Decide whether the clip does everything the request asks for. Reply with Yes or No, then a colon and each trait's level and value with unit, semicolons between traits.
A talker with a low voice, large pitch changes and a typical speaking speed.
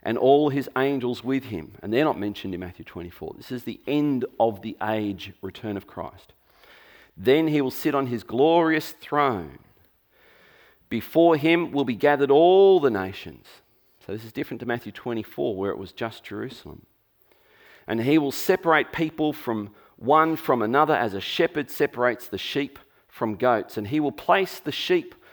Yes: low, 130 Hz; wide, 5.9 semitones; average, 175 wpm